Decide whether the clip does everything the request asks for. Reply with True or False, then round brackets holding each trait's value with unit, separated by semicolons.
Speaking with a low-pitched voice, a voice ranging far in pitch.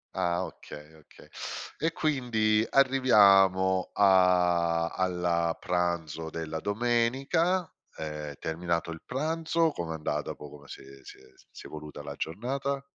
True (90 Hz; 7.2 semitones)